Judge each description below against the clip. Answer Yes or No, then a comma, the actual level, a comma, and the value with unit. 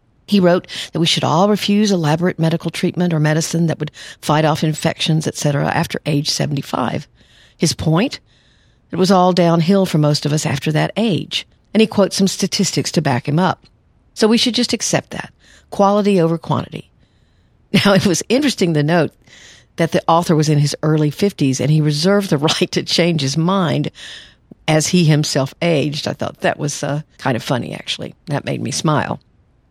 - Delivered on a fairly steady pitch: No, average, 3.9 semitones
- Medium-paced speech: Yes, average, 185 wpm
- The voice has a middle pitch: Yes, medium, 165 Hz